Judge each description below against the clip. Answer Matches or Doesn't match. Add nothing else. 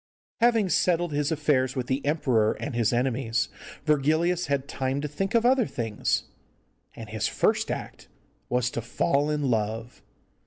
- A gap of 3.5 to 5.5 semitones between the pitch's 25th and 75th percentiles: Matches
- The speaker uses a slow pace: Doesn't match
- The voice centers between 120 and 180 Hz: Matches